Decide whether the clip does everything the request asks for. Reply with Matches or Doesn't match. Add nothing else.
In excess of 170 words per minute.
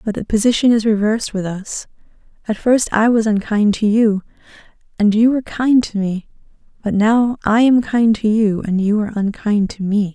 Matches